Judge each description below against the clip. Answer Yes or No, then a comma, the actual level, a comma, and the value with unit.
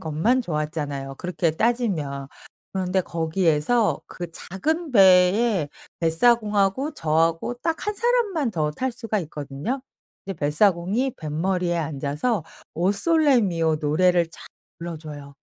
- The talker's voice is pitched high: No, medium, 180 Hz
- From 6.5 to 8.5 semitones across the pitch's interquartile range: Yes, wide, 6.9 semitones